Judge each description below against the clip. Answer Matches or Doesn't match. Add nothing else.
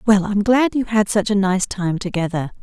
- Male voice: Doesn't match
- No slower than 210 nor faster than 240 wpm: Matches